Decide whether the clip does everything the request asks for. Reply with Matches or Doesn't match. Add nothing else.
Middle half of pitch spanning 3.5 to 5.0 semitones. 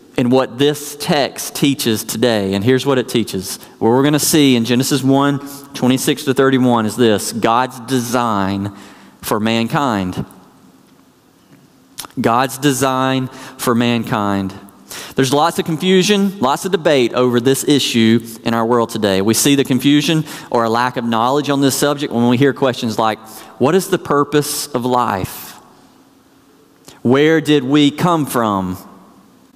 Matches